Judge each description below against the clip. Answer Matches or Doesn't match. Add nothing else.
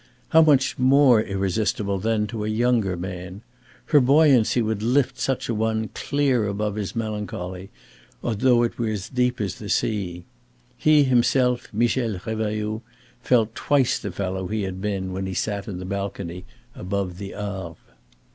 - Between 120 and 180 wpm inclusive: Matches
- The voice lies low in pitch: Matches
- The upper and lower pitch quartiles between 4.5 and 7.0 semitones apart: Doesn't match